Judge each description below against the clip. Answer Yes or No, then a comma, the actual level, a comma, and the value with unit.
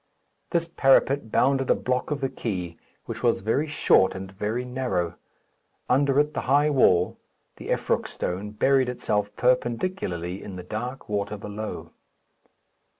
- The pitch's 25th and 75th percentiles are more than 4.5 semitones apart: Yes, average, 5.2 semitones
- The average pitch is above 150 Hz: No, low, 120 Hz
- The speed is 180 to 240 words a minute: No, average, 145 wpm